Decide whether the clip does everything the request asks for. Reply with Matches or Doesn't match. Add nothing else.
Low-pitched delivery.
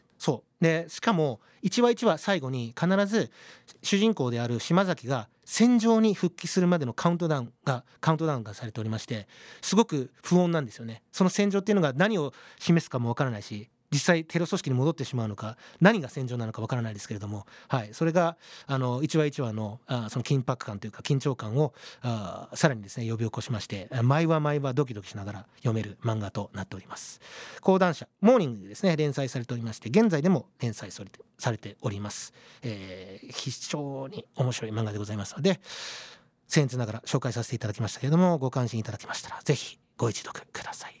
Matches